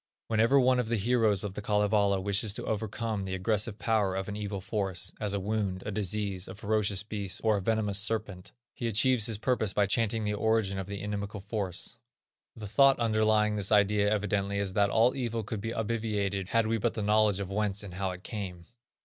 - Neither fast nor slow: No, fast, 210 wpm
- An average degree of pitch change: No, narrow, 1.9 semitones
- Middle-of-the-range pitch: No, low, 105 Hz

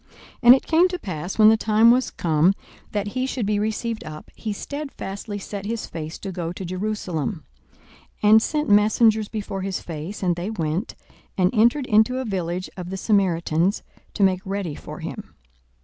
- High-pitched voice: Yes, high, 205 Hz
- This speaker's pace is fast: No, average, 185 wpm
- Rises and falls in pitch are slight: No, average, 3.6 semitones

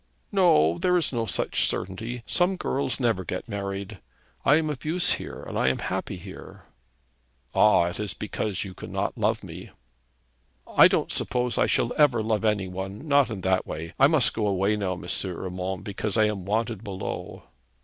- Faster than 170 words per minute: Yes, average, 180 wpm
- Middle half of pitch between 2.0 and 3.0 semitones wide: No, average, 4.7 semitones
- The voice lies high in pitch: No, low, 105 Hz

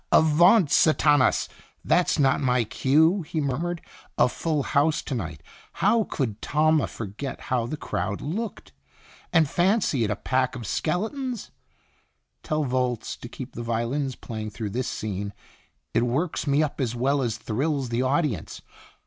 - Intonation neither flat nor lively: Yes, average, 5.0 semitones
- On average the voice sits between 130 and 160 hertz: Yes, low, 135 Hz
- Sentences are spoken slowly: No, average, 150 wpm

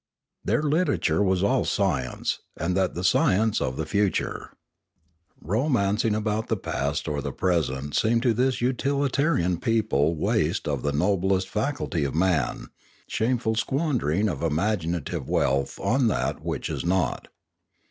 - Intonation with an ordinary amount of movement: No, wide, 6.3 semitones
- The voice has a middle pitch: No, very low, 95 Hz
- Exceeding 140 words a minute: No, slow, 135 wpm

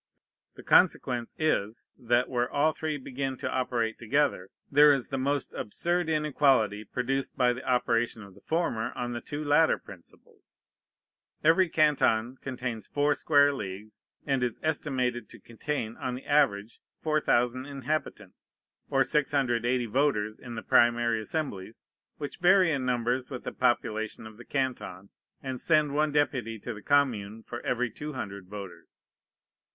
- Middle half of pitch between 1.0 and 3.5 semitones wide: No, average, 4.1 semitones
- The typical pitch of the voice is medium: No, low, 125 Hz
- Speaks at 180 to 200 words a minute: No, average, 145 wpm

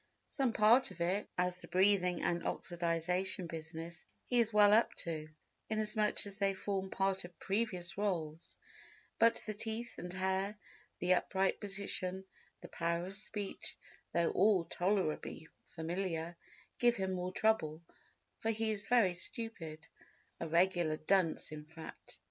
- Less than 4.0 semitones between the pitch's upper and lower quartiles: Yes, average, 3.4 semitones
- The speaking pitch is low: No, high, 190 Hz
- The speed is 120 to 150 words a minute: Yes, slow, 135 wpm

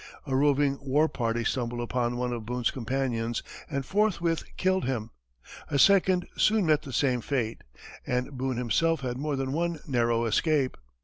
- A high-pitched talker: No, low, 135 Hz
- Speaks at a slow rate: No, average, 165 wpm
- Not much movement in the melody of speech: No, average, 4.2 semitones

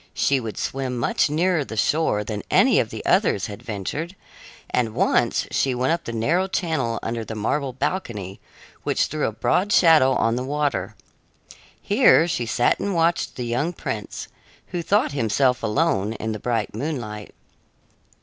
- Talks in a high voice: No, low, 125 Hz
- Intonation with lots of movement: Yes, wide, 6.4 semitones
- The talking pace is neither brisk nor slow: Yes, average, 165 wpm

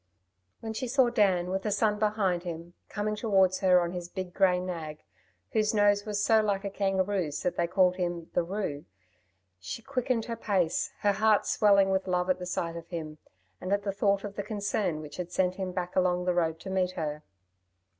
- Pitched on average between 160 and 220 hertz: Yes, high, 190 Hz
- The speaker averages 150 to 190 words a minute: No, fast, 205 wpm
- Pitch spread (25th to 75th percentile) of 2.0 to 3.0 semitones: Yes, average, 2.7 semitones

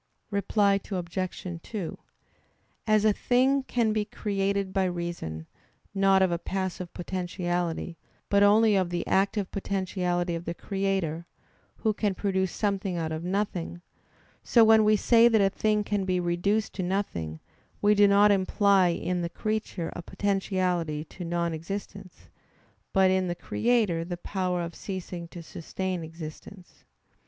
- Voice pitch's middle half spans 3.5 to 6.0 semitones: No, average, 2.7 semitones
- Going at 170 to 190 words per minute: No, average, 145 wpm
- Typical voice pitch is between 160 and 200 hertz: Yes, high, 190 Hz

